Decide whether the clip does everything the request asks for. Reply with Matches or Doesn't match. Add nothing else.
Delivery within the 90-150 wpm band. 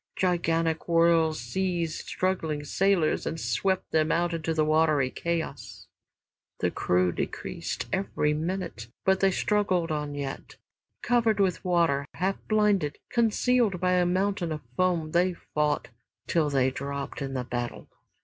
Matches